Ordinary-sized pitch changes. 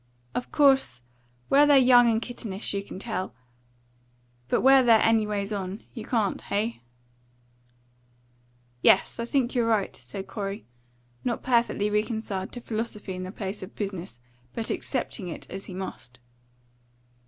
Yes: average, 3.6 semitones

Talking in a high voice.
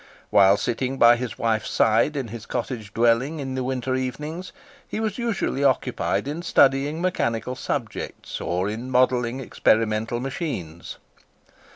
No: low, 125 Hz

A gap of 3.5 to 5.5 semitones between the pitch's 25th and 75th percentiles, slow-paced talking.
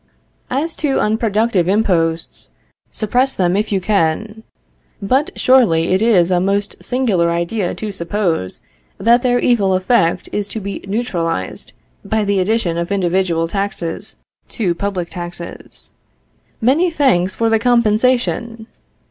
Yes: average, 4.7 semitones; slow, 130 wpm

